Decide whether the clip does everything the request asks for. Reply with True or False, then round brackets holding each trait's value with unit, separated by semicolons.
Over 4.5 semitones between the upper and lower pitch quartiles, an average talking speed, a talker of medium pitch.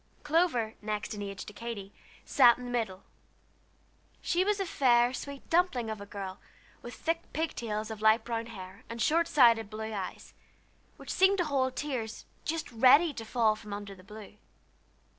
False (5.0 semitones; 180 wpm; 230 Hz)